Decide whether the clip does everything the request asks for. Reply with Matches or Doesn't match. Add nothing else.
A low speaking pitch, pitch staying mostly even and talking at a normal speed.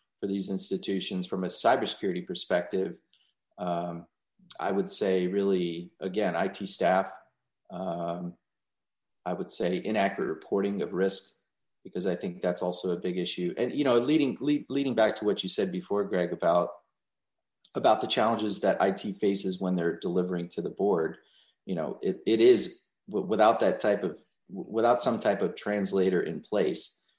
Matches